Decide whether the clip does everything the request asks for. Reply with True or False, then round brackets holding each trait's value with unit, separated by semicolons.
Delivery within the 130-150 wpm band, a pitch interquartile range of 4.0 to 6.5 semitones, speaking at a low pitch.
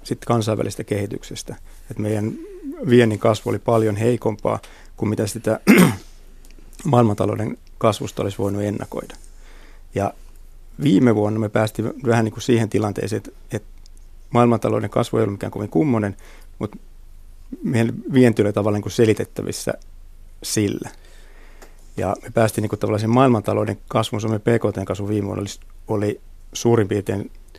False (135 wpm; 3.4 semitones; 105 Hz)